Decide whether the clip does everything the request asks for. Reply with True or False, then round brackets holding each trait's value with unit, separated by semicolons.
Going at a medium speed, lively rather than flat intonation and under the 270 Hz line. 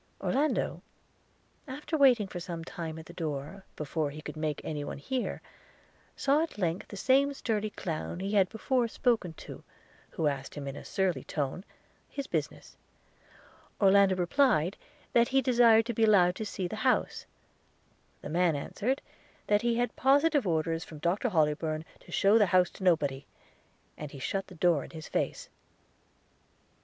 True (170 wpm; 6.8 semitones; 185 Hz)